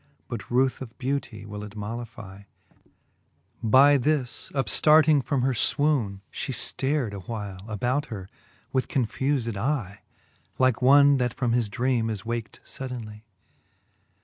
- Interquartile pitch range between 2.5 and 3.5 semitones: No, average, 4.0 semitones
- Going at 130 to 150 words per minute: Yes, slow, 135 wpm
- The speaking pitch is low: Yes, low, 120 Hz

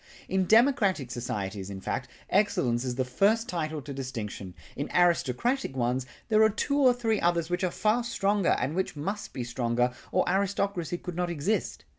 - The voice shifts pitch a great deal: Yes, wide, 8.4 semitones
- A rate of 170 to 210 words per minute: Yes, average, 175 wpm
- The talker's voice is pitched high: No, medium, 175 Hz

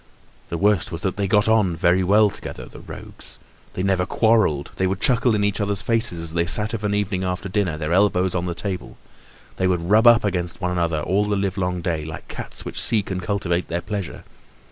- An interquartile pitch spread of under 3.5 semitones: Yes, average, 2.9 semitones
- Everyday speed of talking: No, fast, 225 wpm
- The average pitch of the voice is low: Yes, very low, 95 Hz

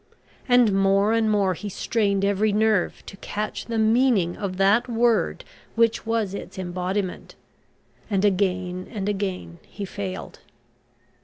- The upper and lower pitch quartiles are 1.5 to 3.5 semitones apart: Yes, narrow, 2.5 semitones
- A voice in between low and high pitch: No, high, 200 Hz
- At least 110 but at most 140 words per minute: Yes, slow, 135 wpm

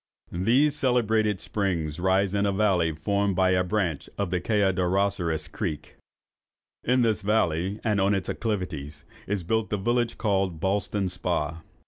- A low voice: Yes, low, 100 Hz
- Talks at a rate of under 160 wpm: Yes, average, 145 wpm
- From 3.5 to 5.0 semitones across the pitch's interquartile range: No, average, 3.1 semitones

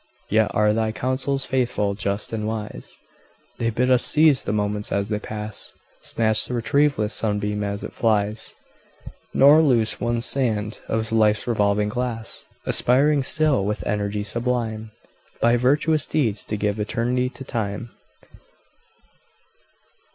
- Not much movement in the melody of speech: No, average, 3.1 semitones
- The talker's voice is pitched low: Yes, low, 110 Hz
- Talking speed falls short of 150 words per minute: Yes, slow, 135 wpm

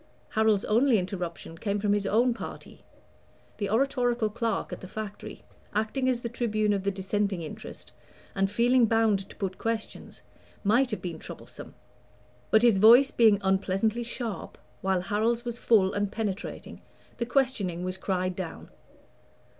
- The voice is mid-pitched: No, high, 215 Hz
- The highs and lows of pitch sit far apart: No, average, 3.3 semitones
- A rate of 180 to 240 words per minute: No, average, 150 wpm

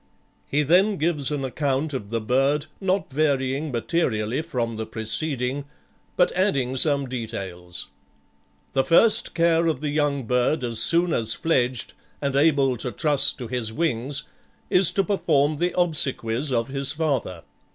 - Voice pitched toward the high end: No, medium, 140 Hz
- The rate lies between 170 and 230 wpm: No, average, 150 wpm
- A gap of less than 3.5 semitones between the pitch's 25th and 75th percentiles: No, average, 4.3 semitones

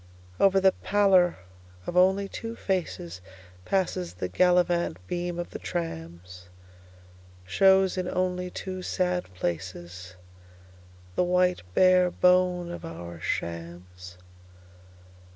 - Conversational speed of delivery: No, slow, 95 wpm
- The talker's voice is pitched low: No, medium, 175 Hz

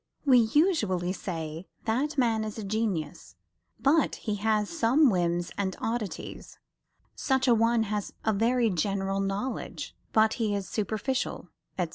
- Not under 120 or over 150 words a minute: Yes, average, 140 wpm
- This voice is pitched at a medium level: No, high, 220 Hz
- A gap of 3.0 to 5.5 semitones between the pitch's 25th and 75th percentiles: Yes, average, 3.6 semitones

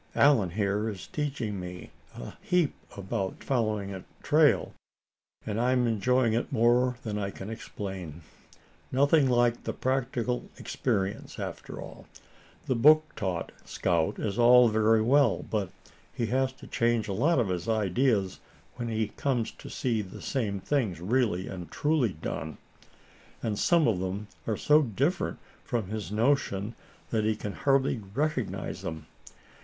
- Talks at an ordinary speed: Yes, average, 150 wpm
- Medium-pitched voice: No, low, 110 Hz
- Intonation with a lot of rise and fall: No, average, 4.6 semitones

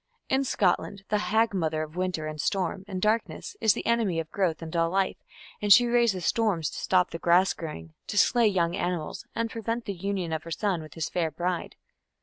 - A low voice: No, medium, 185 Hz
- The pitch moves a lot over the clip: No, average, 4.2 semitones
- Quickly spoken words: Yes, fast, 210 wpm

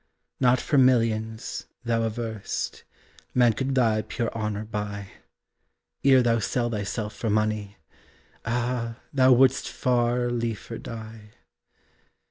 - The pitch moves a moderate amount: No, narrow, 2.2 semitones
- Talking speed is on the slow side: Yes, slow, 110 wpm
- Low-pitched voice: Yes, low, 115 Hz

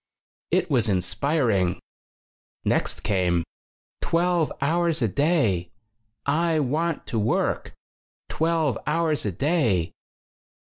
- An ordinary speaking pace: No, slow, 95 wpm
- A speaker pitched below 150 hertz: Yes, medium, 140 Hz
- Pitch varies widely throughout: Yes, wide, 8.3 semitones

